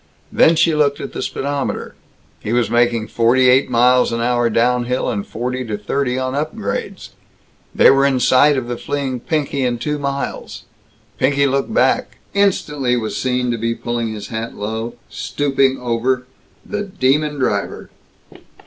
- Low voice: Yes, low, 125 Hz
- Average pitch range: Yes, average, 3.0 semitones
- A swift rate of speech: No, average, 160 wpm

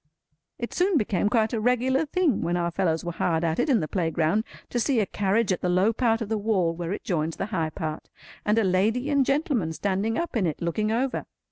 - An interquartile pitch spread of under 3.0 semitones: No, wide, 5.6 semitones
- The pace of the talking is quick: Yes, fast, 235 wpm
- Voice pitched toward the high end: Yes, high, 205 Hz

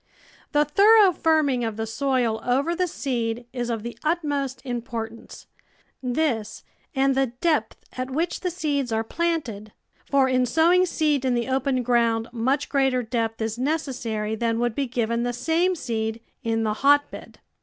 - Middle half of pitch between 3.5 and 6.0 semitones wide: Yes, average, 4.2 semitones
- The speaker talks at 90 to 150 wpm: No, average, 165 wpm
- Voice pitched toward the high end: Yes, very high, 255 Hz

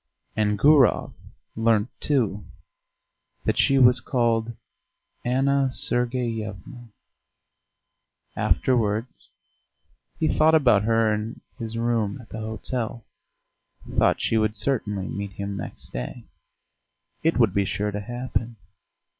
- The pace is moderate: No, slow, 110 wpm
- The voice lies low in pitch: Yes, low, 115 Hz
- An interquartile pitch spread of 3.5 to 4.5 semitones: No, average, 3.0 semitones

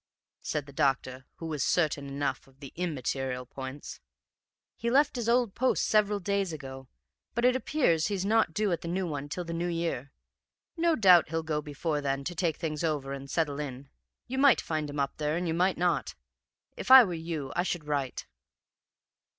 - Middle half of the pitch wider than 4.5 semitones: Yes, average, 5.2 semitones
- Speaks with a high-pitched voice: No, medium, 160 Hz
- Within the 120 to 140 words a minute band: No, average, 200 wpm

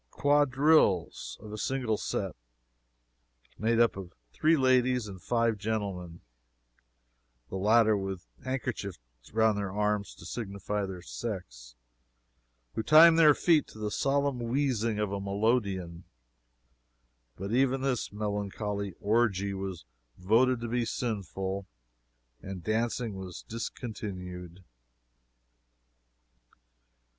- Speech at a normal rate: No, slow, 110 wpm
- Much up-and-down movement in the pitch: No, average, 4.1 semitones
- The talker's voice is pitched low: Yes, low, 105 Hz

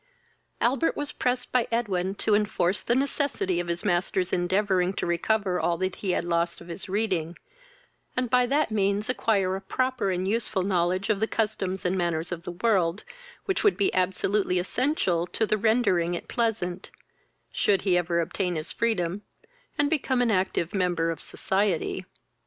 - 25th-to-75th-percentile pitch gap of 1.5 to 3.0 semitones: No, average, 4.0 semitones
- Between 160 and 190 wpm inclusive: Yes, average, 170 wpm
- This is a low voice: No, high, 190 Hz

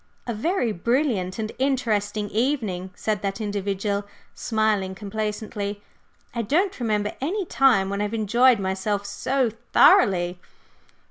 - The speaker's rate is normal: No, slow, 125 wpm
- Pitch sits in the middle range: No, high, 210 Hz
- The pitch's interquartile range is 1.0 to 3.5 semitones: Yes, average, 3.2 semitones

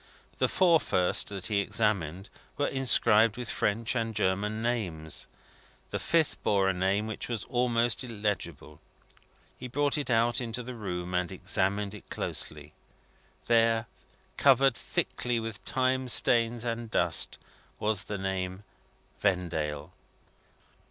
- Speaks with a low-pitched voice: Yes, low, 110 Hz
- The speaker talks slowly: Yes, slow, 130 wpm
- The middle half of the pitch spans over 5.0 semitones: No, average, 4.1 semitones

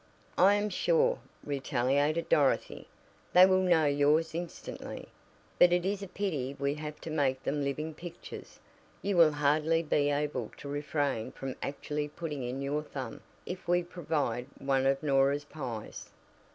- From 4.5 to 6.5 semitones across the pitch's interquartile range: No, average, 3.5 semitones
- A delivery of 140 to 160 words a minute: Yes, average, 150 wpm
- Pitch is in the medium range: Yes, medium, 150 Hz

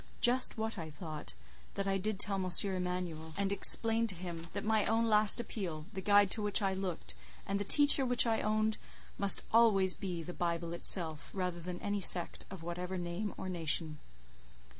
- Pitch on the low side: No, high, 190 Hz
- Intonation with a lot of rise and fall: No, average, 3.6 semitones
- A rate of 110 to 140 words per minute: No, average, 185 wpm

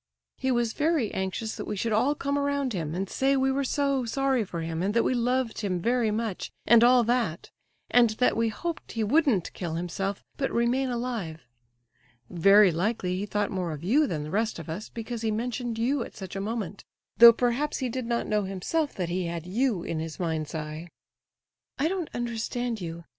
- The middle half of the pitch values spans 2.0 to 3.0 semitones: No, wide, 5.5 semitones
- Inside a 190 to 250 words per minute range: Yes, fast, 205 wpm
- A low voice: No, high, 225 Hz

